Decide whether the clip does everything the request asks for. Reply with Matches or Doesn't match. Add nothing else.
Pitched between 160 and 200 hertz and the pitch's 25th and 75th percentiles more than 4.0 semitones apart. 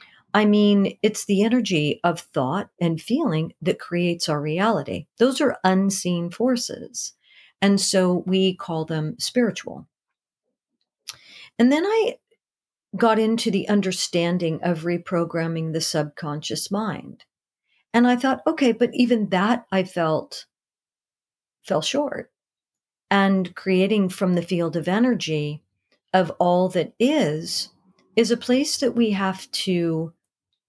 Matches